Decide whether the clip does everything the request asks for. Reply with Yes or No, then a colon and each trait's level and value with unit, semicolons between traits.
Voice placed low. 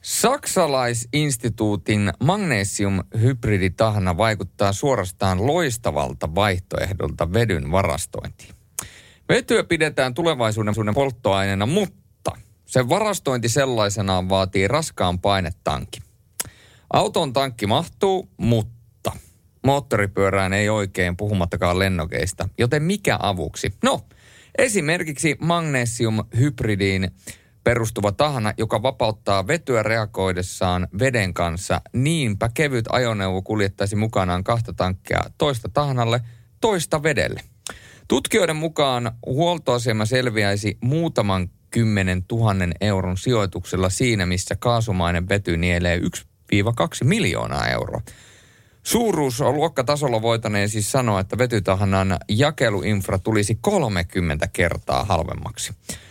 Yes: low, 105 Hz